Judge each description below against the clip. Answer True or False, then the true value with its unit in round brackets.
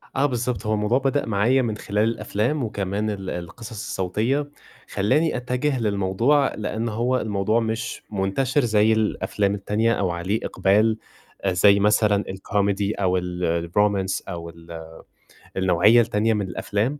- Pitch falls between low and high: False (105 Hz)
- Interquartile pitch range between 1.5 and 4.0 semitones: True (3.2 semitones)